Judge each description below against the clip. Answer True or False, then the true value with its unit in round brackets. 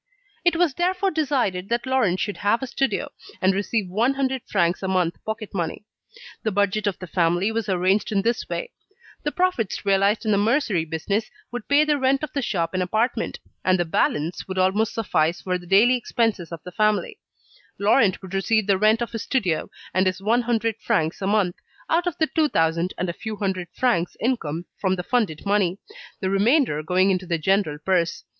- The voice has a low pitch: False (200 Hz)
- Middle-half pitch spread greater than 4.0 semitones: True (4.5 semitones)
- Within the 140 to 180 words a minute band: False (200 wpm)